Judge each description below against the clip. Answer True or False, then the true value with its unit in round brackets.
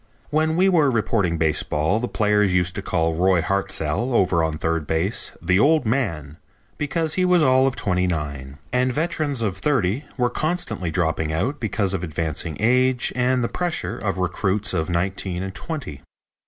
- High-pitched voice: False (100 Hz)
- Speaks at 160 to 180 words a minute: True (170 wpm)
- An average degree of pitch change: False (7.4 semitones)